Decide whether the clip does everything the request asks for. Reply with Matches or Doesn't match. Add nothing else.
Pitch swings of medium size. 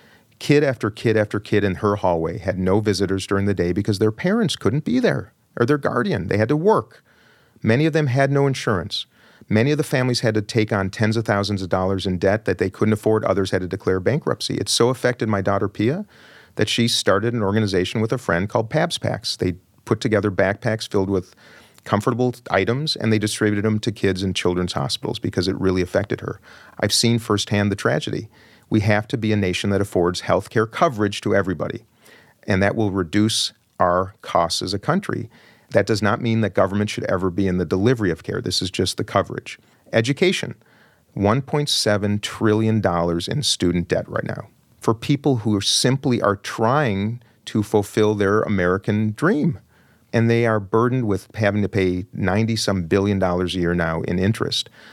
Matches